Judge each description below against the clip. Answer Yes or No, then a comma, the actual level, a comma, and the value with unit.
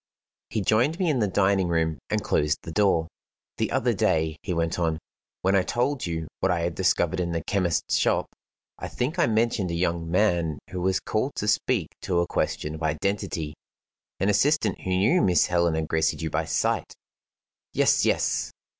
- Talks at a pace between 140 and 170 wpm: No, average, 180 wpm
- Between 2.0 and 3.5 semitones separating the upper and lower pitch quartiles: No, average, 4.2 semitones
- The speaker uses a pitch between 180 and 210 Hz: No, very low, 90 Hz